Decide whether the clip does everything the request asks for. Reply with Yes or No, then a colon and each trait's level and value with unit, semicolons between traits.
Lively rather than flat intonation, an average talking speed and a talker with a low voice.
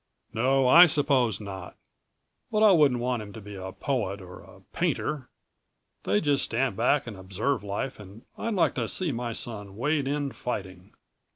Yes: wide, 5.8 semitones; average, 175 wpm; low, 120 Hz